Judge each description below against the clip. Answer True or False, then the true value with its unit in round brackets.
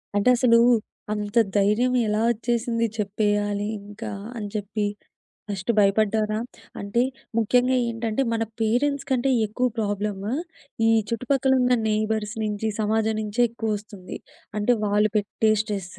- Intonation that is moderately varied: False (2.0 semitones)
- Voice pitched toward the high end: True (215 Hz)